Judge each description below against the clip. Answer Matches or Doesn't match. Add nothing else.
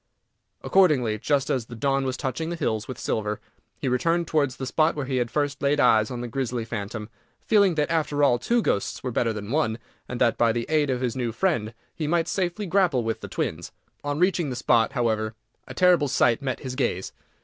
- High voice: Doesn't match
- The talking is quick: Matches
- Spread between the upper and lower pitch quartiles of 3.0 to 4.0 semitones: Doesn't match